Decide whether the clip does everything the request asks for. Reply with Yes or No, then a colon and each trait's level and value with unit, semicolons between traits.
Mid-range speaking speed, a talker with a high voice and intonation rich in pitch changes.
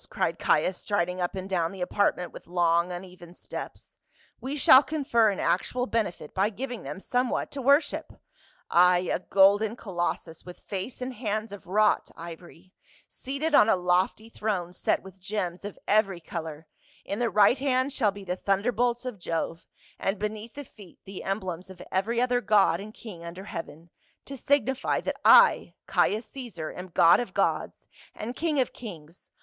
No: average, 175 wpm; high, 200 Hz; average, 5.0 semitones